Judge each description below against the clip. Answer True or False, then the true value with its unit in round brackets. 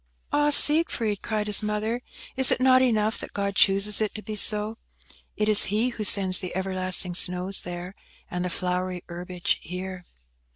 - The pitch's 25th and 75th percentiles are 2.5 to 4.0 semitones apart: True (2.9 semitones)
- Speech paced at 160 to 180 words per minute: True (170 wpm)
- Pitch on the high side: True (200 Hz)